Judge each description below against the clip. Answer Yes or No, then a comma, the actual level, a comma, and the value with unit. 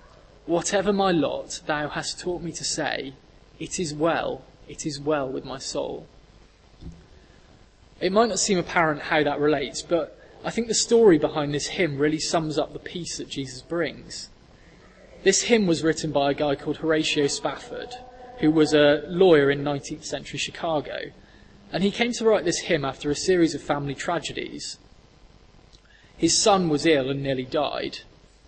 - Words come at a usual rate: Yes, average, 170 wpm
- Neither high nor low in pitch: Yes, medium, 155 Hz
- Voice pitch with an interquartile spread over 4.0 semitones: No, average, 3.3 semitones